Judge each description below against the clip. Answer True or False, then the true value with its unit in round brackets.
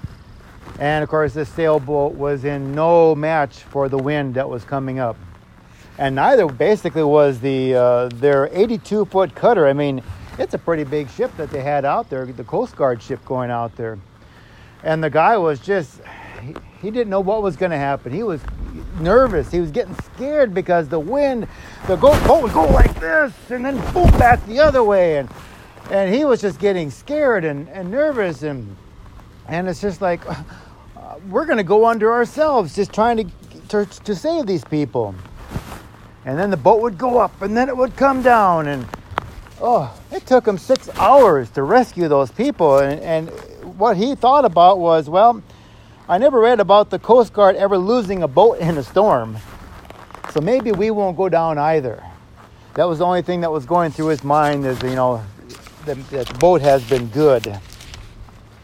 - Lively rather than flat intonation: True (8.0 semitones)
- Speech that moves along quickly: False (185 wpm)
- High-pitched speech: False (155 Hz)